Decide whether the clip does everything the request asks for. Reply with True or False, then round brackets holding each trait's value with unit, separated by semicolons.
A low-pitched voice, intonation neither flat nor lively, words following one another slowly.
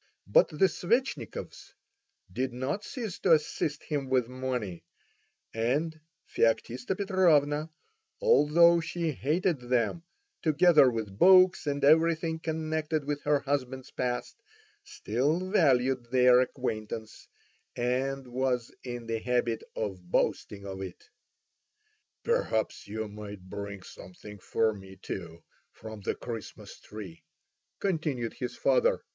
False (130 Hz; 6.0 semitones; 115 wpm)